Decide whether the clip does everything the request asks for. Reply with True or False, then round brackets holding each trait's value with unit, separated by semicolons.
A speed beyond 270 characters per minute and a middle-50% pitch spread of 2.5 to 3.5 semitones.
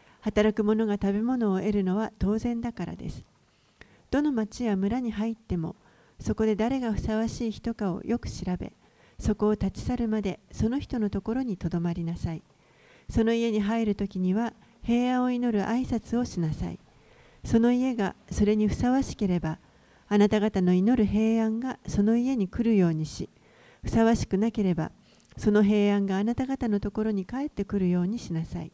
True (335 characters per minute; 2.9 semitones)